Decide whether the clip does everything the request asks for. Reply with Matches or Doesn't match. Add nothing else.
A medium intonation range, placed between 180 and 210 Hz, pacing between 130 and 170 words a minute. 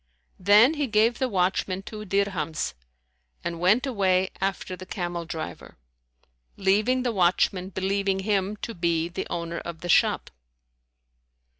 Matches